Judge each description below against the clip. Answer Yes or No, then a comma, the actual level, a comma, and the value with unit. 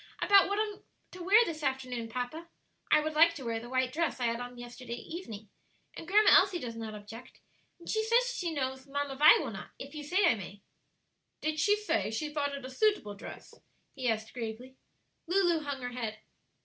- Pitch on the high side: Yes, very high, 280 Hz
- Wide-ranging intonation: Yes, wide, 6.0 semitones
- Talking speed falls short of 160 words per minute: No, fast, 205 wpm